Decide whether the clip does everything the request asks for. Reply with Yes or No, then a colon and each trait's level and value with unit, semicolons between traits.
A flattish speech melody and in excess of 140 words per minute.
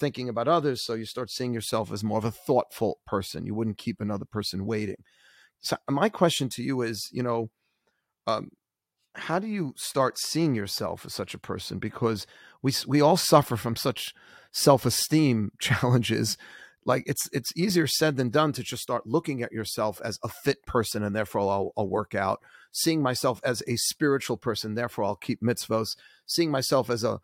No: average, 4.1 semitones; average, 190 wpm